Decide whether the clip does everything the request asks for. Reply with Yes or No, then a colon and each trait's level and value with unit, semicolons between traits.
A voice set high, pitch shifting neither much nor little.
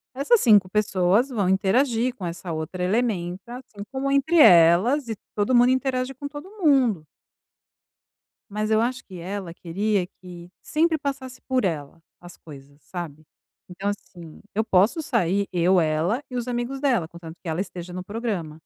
No: high, 205 Hz; wide, 6.3 semitones